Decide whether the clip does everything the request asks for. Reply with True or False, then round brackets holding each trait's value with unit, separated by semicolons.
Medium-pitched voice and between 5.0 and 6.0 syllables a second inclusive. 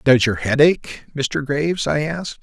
False (145 Hz; 4.6 syllables/s)